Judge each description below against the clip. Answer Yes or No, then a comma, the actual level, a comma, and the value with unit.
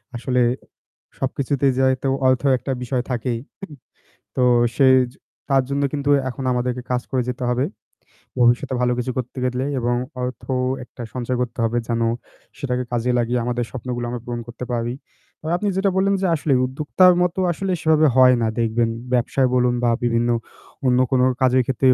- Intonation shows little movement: Yes, narrow, 1.7 semitones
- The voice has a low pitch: Yes, low, 125 Hz